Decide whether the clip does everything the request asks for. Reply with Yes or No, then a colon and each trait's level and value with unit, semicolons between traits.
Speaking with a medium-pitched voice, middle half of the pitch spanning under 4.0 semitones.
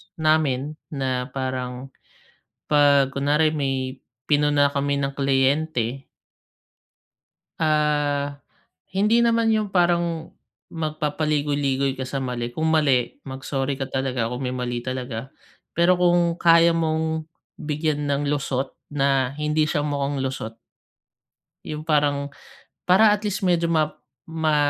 Yes: medium, 145 Hz; average, 2.9 semitones